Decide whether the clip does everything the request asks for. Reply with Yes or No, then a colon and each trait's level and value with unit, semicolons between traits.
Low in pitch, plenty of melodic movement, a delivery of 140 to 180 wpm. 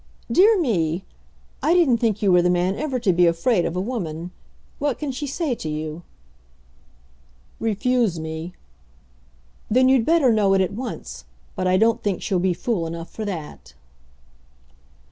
No: high, 200 Hz; wide, 6.4 semitones; average, 165 wpm